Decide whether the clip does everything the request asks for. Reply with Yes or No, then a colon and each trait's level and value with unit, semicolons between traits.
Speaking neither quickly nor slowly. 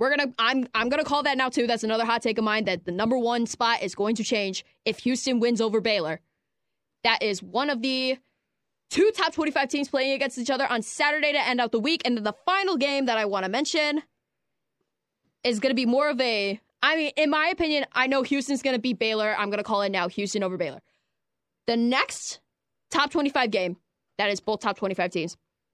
No: fast, 235 wpm